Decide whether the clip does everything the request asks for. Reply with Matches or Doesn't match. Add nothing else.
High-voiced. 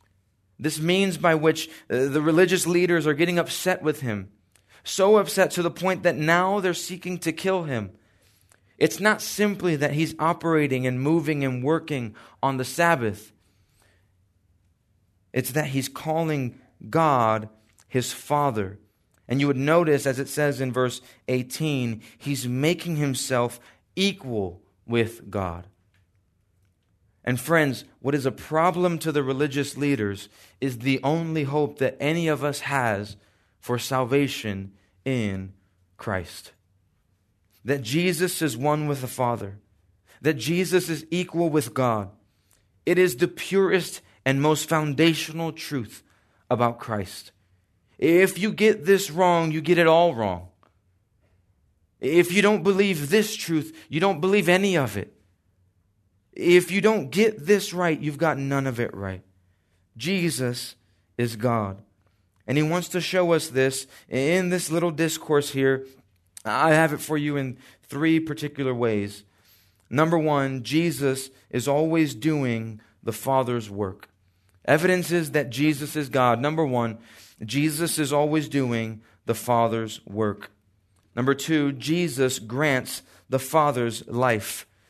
Doesn't match